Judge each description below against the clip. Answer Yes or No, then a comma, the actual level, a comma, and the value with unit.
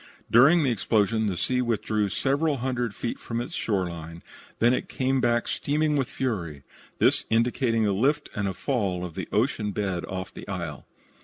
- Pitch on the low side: Yes, low, 115 Hz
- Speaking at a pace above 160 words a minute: Yes, average, 175 wpm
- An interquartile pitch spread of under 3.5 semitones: No, average, 5.1 semitones